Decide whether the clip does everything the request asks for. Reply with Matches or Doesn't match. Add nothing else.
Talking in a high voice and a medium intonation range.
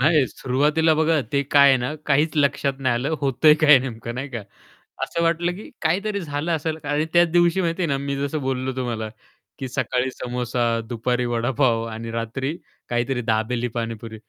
Doesn't match